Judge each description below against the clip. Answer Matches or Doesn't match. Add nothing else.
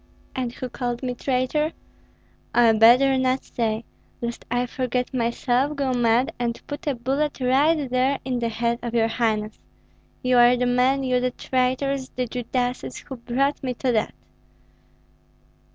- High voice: Matches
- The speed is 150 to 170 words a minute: Matches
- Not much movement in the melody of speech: Matches